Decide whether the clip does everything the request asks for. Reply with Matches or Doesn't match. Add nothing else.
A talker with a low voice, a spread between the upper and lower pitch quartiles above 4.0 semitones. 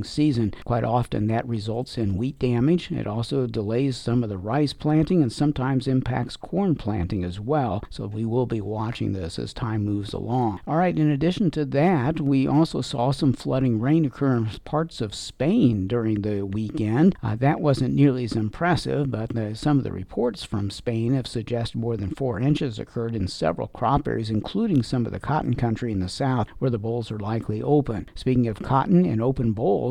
Matches